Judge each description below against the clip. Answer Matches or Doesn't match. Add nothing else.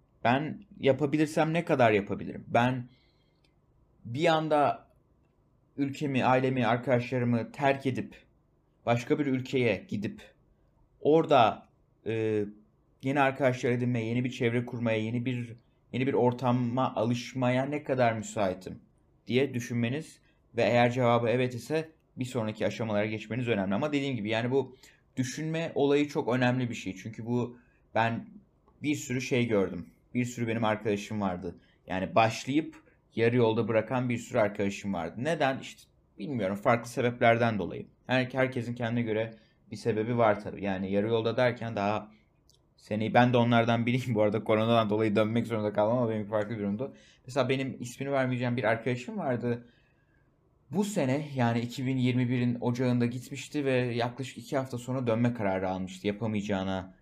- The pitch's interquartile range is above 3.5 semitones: Doesn't match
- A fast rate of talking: Matches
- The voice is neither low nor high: Doesn't match